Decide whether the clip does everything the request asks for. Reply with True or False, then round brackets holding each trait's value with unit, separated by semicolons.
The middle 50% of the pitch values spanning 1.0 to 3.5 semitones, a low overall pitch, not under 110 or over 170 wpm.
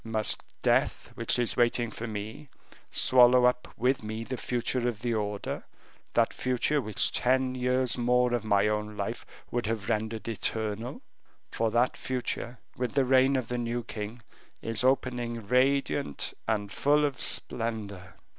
True (2.6 semitones; 120 Hz; 155 wpm)